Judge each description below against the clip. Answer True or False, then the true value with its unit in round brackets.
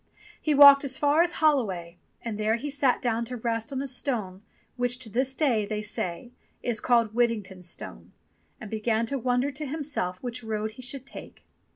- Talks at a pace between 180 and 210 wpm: True (195 wpm)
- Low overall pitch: False (240 Hz)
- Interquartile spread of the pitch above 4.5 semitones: False (3.9 semitones)